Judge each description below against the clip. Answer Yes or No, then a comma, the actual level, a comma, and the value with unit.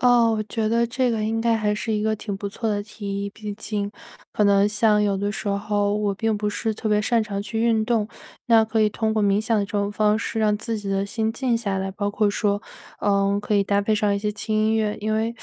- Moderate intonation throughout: No, narrow, 1.6 semitones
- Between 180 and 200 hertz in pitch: No, high, 210 Hz